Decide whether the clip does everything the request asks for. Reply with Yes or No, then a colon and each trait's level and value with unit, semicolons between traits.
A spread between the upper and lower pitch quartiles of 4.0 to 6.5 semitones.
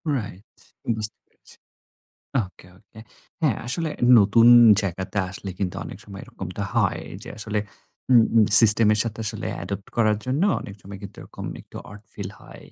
No: narrow, 2.6 semitones